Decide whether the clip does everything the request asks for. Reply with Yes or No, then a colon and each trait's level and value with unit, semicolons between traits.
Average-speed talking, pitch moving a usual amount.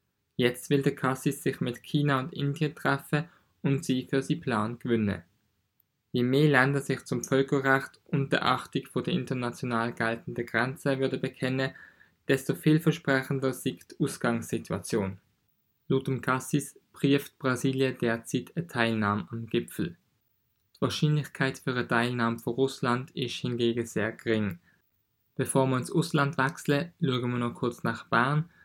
Yes: average, 140 wpm; average, 3.0 semitones